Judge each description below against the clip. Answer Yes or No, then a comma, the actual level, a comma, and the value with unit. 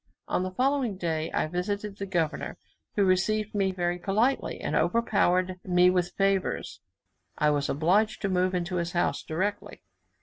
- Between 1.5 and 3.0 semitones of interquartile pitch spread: Yes, narrow, 2.5 semitones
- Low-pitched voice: No, medium, 185 Hz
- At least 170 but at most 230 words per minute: No, average, 160 wpm